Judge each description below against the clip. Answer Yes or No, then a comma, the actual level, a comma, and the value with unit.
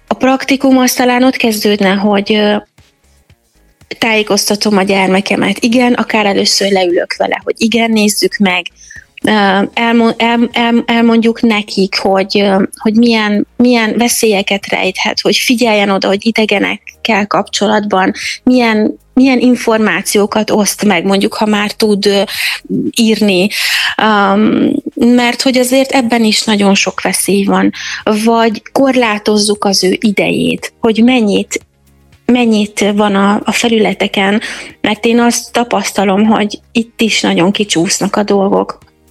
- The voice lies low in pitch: No, high, 215 Hz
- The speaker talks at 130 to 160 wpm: No, average, 115 wpm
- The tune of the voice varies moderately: Yes, average, 3.0 semitones